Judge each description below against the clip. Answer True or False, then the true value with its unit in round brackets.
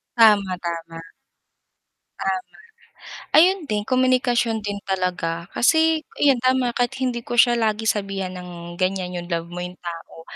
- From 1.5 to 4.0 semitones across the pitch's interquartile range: False (5.5 semitones)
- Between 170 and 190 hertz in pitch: False (200 Hz)